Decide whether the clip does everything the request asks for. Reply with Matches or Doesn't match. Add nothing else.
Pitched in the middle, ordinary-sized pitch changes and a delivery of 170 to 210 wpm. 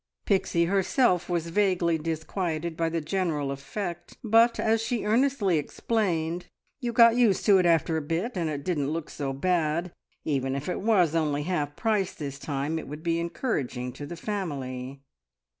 Matches